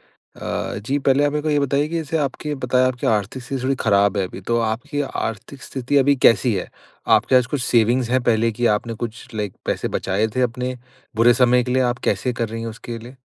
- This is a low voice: Yes, low, 125 Hz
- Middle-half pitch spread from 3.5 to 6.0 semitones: No, average, 2.9 semitones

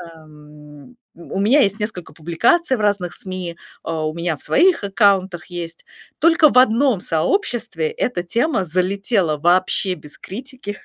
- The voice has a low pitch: No, medium, 185 Hz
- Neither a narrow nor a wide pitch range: No, wide, 5.8 semitones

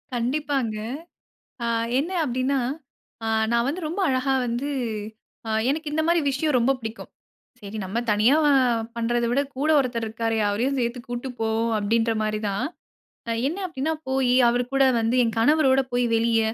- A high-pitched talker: Yes, high, 245 Hz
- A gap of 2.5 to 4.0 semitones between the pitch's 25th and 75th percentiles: Yes, average, 3.4 semitones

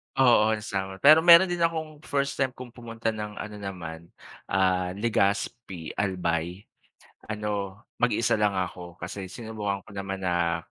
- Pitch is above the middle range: No, low, 105 Hz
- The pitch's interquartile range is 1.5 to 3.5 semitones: No, average, 4.1 semitones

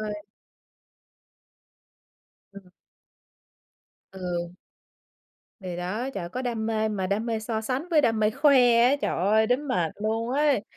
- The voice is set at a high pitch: Yes, high, 220 Hz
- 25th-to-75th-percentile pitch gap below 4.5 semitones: Yes, average, 3.9 semitones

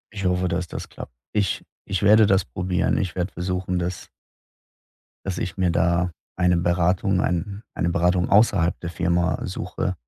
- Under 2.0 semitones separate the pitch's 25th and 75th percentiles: Yes, narrow, 1.5 semitones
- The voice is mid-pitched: No, very low, 90 Hz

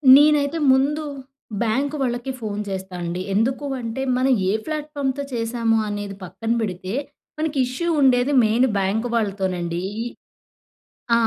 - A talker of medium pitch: No, high, 235 Hz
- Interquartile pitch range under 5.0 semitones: No, average, 5.3 semitones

